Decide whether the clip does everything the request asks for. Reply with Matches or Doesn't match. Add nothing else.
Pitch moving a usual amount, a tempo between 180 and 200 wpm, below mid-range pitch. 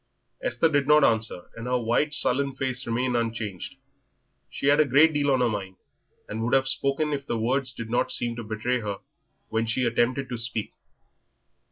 Matches